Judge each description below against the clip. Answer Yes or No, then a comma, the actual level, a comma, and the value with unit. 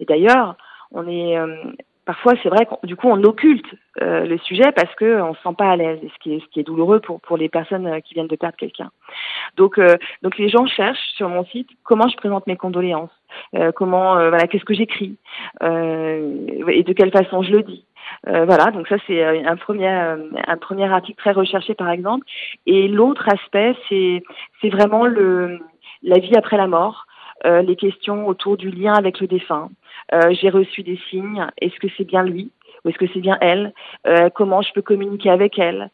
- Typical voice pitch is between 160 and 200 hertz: Yes, high, 190 Hz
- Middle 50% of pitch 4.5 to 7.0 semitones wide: No, average, 3.1 semitones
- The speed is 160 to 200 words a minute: No, average, 210 wpm